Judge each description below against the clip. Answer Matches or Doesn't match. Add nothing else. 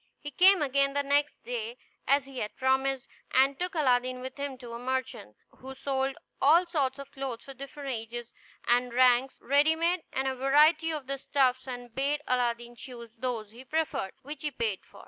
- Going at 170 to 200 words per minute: Matches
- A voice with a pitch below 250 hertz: Doesn't match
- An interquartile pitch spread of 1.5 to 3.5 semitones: Matches